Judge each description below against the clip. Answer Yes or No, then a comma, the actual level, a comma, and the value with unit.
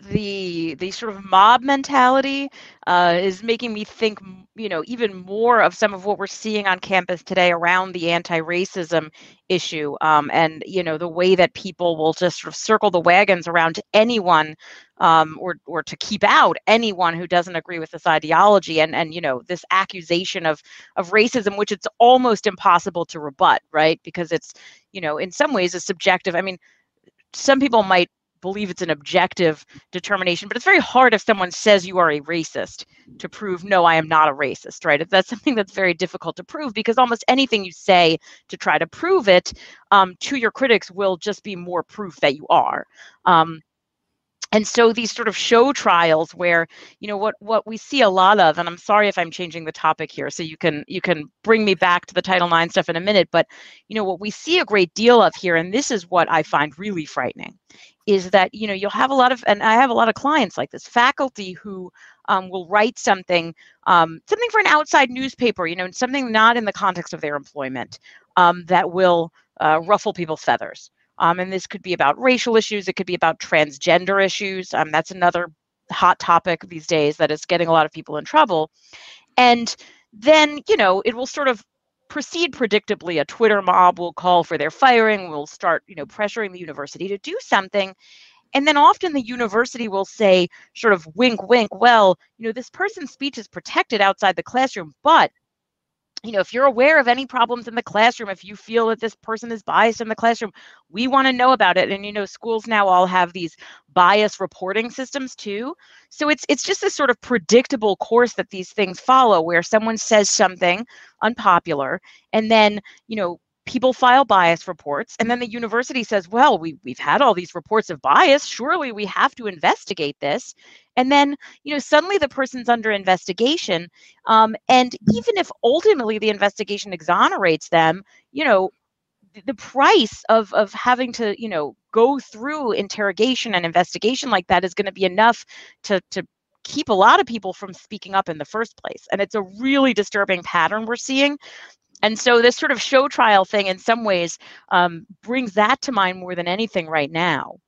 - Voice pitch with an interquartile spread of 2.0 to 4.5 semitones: No, average, 5.0 semitones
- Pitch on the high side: Yes, high, 200 Hz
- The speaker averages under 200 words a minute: No, fast, 205 wpm